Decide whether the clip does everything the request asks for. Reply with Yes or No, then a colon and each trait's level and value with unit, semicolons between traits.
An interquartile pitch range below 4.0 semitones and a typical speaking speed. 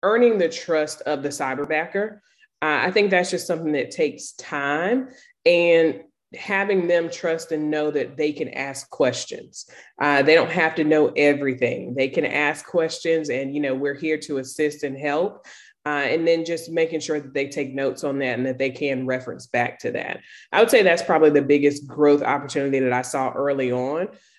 Yes: average, 3.0 semitones; average, 195 wpm